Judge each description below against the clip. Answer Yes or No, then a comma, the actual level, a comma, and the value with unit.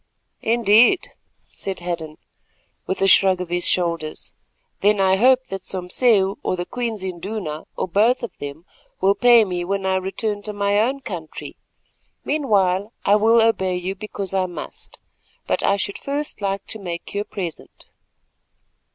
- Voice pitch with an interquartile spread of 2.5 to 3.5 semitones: Yes, average, 3.2 semitones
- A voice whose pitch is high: Yes, high, 195 Hz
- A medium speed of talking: Yes, average, 160 wpm